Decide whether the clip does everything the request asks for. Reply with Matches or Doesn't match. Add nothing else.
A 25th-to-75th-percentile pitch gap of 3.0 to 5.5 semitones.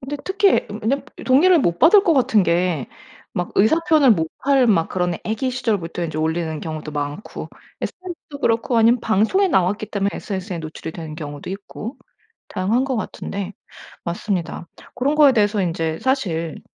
Doesn't match